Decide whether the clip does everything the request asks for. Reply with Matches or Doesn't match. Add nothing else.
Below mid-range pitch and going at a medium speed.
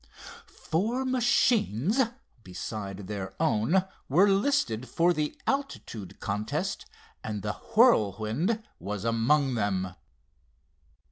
Doesn't match